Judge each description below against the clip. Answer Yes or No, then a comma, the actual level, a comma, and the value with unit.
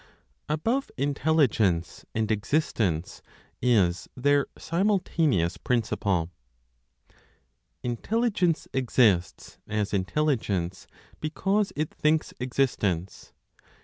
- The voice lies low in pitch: Yes, low, 125 Hz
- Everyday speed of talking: No, slow, 70 wpm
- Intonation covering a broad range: Yes, wide, 7.9 semitones